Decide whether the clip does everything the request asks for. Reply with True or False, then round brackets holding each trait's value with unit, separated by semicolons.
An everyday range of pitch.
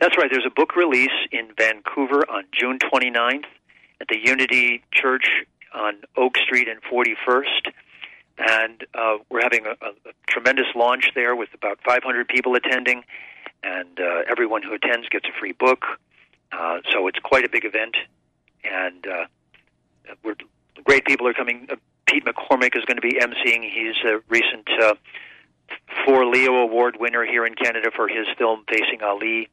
False (2.2 semitones)